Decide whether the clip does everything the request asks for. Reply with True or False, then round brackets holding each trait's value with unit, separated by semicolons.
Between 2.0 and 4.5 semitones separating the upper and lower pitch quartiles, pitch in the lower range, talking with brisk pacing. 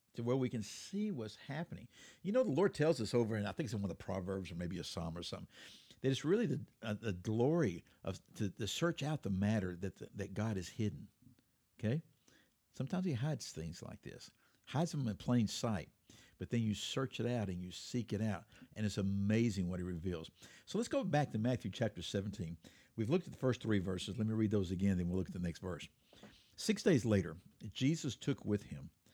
False (5.4 semitones; 110 Hz; 230 wpm)